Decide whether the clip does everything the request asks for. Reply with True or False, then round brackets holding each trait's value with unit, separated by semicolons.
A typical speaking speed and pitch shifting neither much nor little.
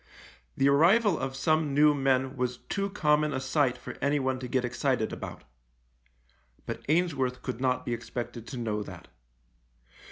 True (160 wpm; 3.4 semitones)